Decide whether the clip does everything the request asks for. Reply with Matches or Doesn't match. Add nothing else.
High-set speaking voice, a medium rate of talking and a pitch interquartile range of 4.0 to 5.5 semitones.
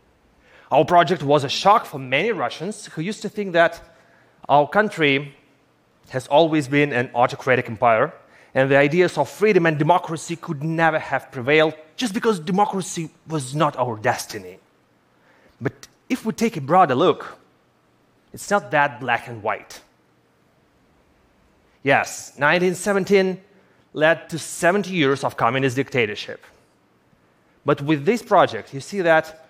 Doesn't match